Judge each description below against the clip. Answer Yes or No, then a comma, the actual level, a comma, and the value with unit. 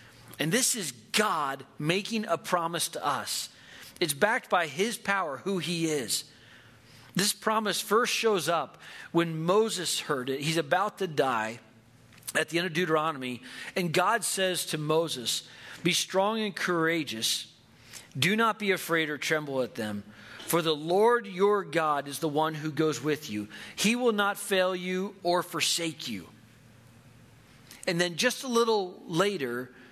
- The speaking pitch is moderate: Yes, medium, 165 Hz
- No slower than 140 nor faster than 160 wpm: Yes, average, 155 wpm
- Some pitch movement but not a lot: No, wide, 6.9 semitones